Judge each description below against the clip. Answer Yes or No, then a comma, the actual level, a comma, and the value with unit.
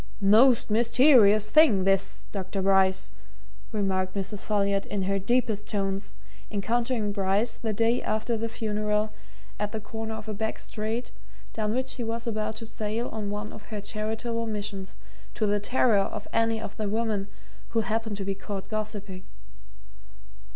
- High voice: Yes, high, 215 Hz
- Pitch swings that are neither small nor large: No, narrow, 2.2 semitones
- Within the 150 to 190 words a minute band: Yes, average, 160 wpm